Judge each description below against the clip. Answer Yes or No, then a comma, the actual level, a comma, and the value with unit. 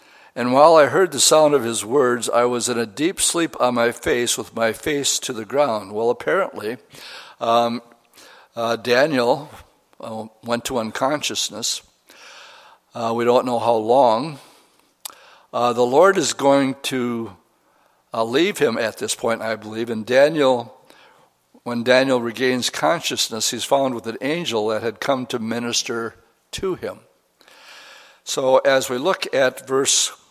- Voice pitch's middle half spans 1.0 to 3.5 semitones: Yes, narrow, 2.6 semitones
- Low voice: Yes, low, 120 Hz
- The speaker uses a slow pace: No, average, 150 wpm